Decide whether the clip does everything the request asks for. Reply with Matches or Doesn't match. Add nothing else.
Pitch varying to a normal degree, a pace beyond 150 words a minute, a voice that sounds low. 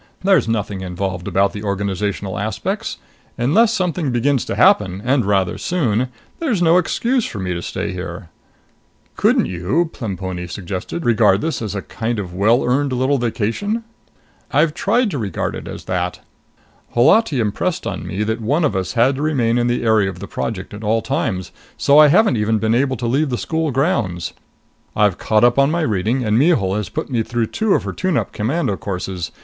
Doesn't match